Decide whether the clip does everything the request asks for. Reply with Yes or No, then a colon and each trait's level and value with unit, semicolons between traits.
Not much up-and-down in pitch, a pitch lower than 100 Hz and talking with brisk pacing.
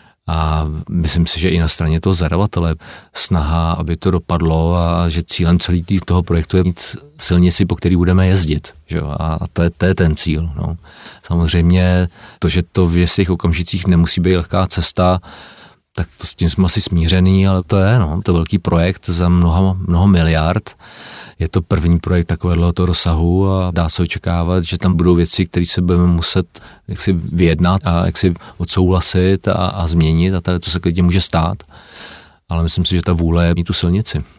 Yes: narrow, 1.6 semitones; very low, 90 Hz; fast, 190 wpm